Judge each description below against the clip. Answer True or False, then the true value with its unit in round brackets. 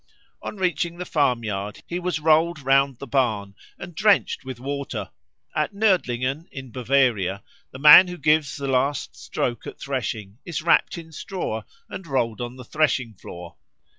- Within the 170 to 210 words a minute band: False (160 wpm)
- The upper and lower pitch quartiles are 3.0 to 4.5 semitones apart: False (5.2 semitones)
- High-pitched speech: False (135 Hz)